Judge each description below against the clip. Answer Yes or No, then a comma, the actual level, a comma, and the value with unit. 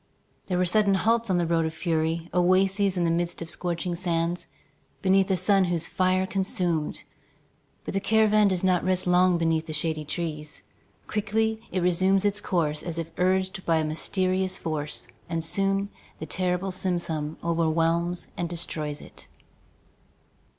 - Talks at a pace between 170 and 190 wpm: No, average, 155 wpm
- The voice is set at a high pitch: No, medium, 180 Hz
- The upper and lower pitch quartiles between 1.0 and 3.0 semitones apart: Yes, narrow, 2.4 semitones